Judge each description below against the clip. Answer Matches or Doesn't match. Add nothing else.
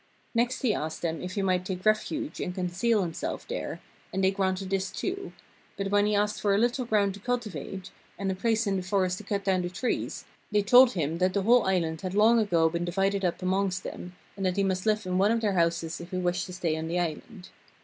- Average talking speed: Doesn't match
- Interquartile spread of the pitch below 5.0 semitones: Matches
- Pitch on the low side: Doesn't match